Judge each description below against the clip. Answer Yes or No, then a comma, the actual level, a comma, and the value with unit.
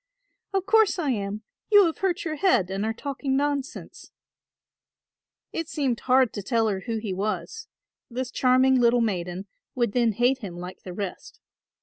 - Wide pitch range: Yes, wide, 5.9 semitones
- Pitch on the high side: Yes, high, 245 Hz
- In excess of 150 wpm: Yes, average, 165 wpm